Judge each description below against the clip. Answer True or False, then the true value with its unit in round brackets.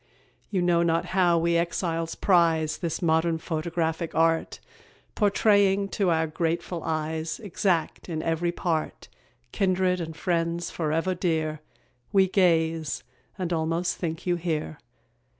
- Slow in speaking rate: True (125 wpm)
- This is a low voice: False (170 Hz)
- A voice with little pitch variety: True (1.9 semitones)